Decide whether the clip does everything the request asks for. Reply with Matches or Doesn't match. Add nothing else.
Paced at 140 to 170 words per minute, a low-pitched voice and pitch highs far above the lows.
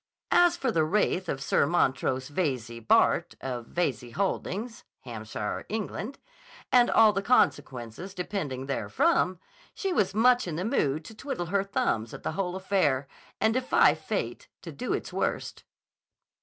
Doesn't match